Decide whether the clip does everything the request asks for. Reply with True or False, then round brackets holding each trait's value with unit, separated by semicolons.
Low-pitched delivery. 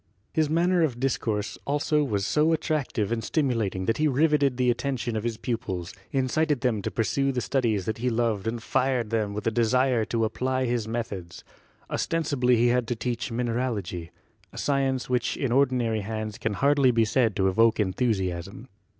True (120 Hz)